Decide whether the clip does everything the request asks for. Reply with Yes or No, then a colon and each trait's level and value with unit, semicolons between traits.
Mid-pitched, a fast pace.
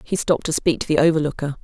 Yes: medium, 160 Hz; fast, 260 wpm